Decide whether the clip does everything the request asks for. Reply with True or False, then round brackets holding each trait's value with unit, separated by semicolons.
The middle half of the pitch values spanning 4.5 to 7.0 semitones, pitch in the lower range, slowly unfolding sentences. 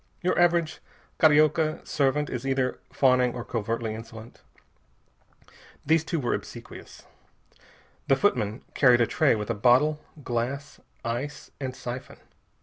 False (4.0 semitones; 130 Hz; 125 wpm)